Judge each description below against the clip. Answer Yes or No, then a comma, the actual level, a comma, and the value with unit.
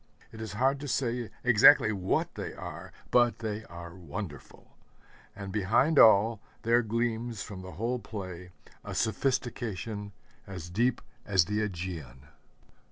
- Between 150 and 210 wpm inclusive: No, slow, 135 wpm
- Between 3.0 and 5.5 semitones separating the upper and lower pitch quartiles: Yes, average, 4.2 semitones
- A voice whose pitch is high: No, low, 105 Hz